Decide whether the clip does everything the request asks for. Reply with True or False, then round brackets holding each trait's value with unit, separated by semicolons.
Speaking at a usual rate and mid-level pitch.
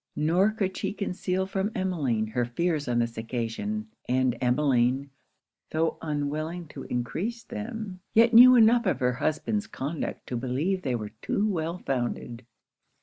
True (145 wpm; 155 Hz)